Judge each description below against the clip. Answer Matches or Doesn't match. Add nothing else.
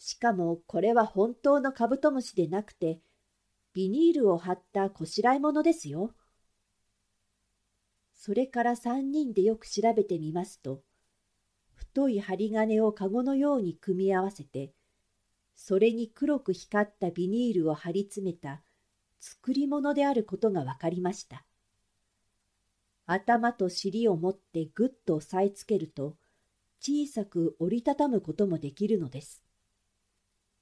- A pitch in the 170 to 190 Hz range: Matches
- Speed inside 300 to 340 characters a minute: Doesn't match